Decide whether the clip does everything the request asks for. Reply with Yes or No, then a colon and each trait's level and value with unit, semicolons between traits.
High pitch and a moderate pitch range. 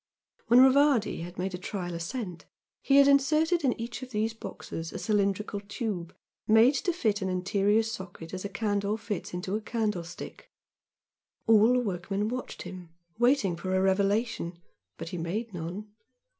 Yes: high, 205 Hz; average, 4.1 semitones